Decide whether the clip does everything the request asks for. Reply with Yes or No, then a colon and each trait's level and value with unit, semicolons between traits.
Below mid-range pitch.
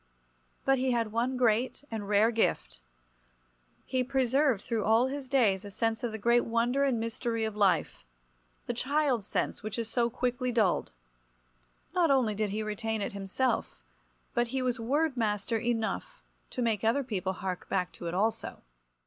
No: high, 230 Hz